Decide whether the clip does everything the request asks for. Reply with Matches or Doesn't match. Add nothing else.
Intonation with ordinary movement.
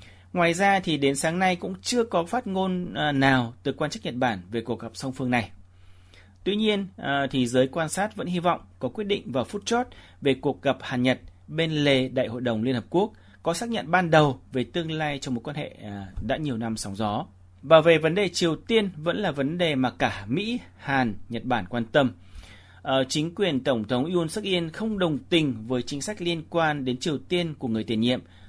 Doesn't match